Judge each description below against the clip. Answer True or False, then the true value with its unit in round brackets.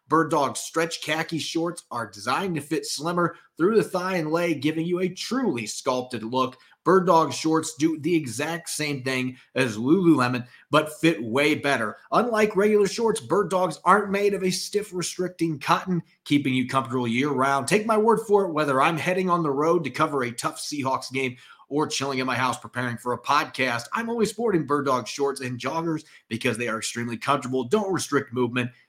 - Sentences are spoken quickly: False (195 wpm)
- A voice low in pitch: False (155 Hz)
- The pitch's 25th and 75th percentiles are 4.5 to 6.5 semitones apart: True (5.3 semitones)